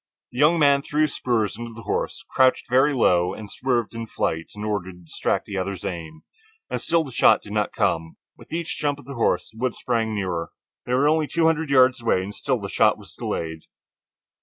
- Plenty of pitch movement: Yes, wide, 6.3 semitones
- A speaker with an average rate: No, fast, 225 wpm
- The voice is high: No, low, 115 Hz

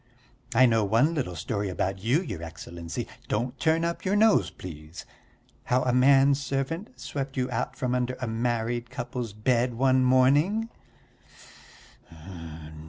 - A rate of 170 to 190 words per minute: No, average, 140 wpm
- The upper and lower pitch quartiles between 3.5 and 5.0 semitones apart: Yes, average, 3.8 semitones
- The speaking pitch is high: No, low, 125 Hz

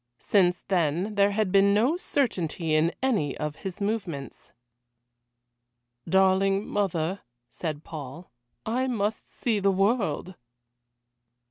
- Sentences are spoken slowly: Yes, slow, 110 wpm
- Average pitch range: Yes, average, 4.0 semitones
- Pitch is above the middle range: Yes, high, 195 Hz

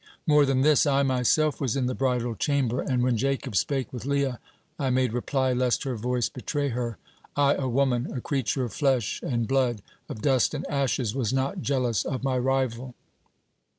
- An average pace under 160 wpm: No, average, 185 wpm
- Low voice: Yes, low, 130 Hz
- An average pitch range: No, narrow, 2.0 semitones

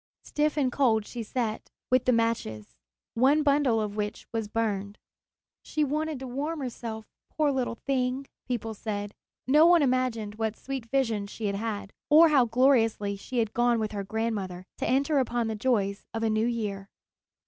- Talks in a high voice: Yes, high, 230 Hz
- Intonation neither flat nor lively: Yes, average, 3.7 semitones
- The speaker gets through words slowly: No, average, 175 wpm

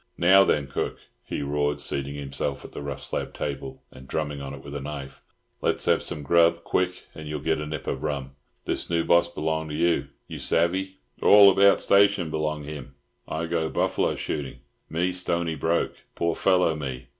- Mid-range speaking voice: No, very low, 80 Hz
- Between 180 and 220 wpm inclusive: Yes, average, 185 wpm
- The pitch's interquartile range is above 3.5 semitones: No, average, 3.2 semitones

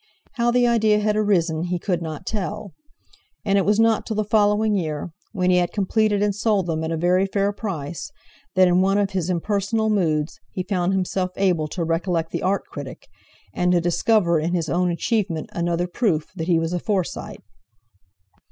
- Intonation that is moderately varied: Yes, average, 3.5 semitones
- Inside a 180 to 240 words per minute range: Yes, average, 190 wpm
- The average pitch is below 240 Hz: Yes, medium, 185 Hz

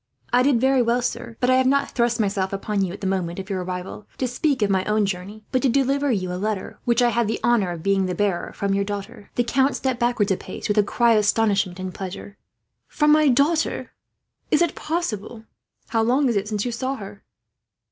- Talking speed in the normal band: No, fast, 240 wpm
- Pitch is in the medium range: No, high, 215 Hz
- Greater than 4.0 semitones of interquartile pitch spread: Yes, average, 4.4 semitones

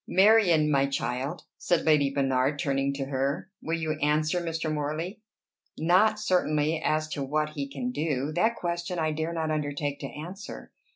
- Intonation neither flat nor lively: Yes, average, 3.2 semitones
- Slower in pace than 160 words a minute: No, average, 165 wpm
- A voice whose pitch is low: No, medium, 155 Hz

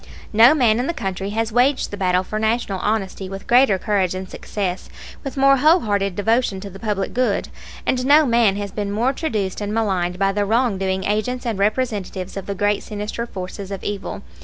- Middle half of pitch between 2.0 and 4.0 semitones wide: Yes, average, 3.5 semitones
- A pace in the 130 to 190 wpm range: No, fast, 205 wpm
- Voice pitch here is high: Yes, high, 205 Hz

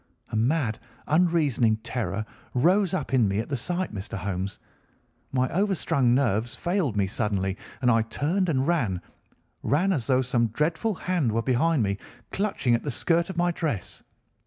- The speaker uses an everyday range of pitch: No, wide, 7.4 semitones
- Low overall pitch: Yes, low, 130 Hz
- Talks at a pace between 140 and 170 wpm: Yes, average, 160 wpm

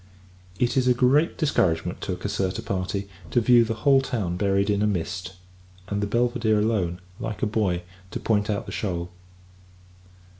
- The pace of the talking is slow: No, average, 175 wpm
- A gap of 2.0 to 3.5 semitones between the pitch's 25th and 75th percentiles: No, average, 4.0 semitones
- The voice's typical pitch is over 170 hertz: No, low, 105 Hz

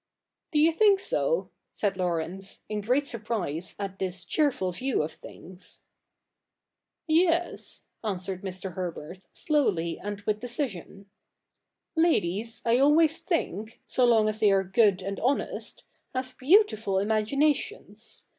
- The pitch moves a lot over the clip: Yes, wide, 7.0 semitones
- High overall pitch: Yes, high, 215 Hz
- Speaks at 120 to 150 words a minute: Yes, slow, 135 wpm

